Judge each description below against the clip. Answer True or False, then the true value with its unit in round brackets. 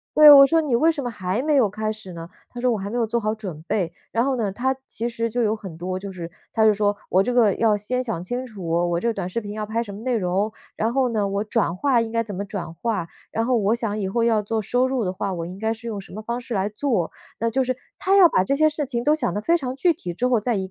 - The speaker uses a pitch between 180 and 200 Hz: False (220 Hz)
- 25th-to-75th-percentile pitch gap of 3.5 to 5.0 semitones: True (3.8 semitones)